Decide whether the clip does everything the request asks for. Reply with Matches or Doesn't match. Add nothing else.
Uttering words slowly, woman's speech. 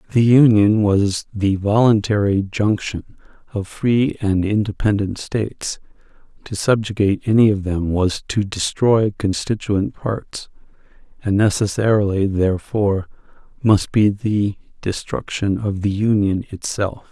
Doesn't match